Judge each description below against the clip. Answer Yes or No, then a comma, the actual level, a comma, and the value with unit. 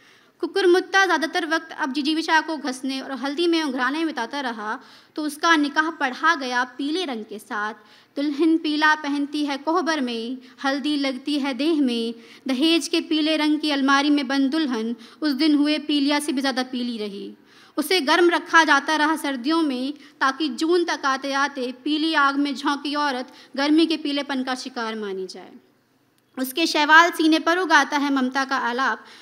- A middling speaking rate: Yes, average, 170 wpm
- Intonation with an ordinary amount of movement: Yes, average, 3.1 semitones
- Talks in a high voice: Yes, very high, 290 Hz